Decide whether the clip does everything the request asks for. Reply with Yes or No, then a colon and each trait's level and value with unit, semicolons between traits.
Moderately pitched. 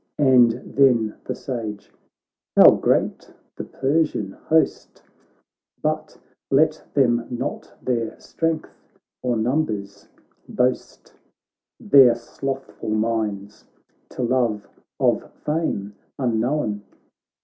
No: low, 120 Hz